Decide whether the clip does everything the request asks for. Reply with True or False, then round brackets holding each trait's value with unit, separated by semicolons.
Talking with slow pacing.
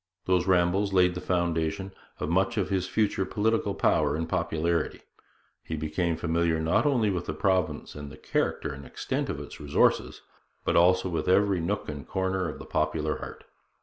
False (180 wpm)